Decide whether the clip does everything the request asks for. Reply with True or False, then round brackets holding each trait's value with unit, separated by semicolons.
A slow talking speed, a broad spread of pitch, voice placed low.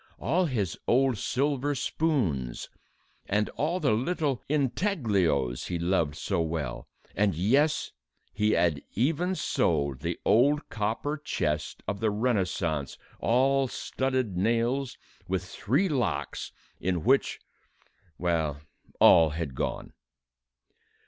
True (110 wpm; 8.5 semitones; 110 Hz)